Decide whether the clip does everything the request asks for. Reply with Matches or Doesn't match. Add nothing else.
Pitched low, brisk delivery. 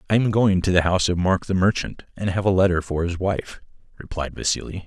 Matches